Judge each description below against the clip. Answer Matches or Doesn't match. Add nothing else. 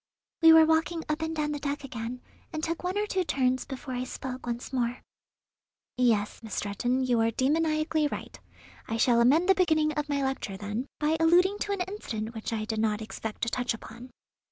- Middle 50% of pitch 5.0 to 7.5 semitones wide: Matches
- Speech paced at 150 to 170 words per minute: Doesn't match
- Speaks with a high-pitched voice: Matches